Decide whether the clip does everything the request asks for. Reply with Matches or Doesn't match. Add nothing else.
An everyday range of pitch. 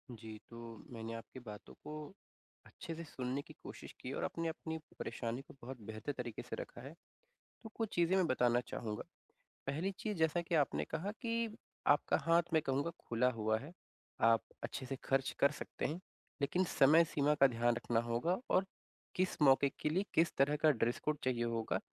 Doesn't match